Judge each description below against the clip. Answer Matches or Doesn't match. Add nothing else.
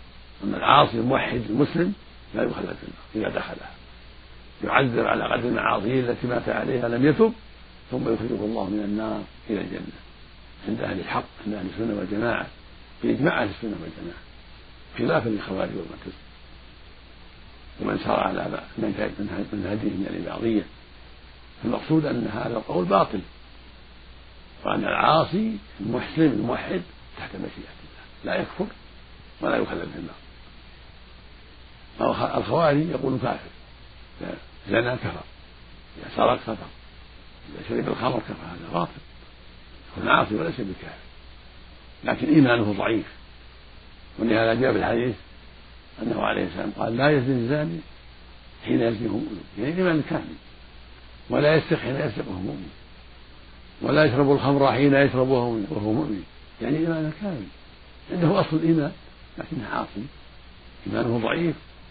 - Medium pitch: Doesn't match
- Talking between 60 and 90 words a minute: Doesn't match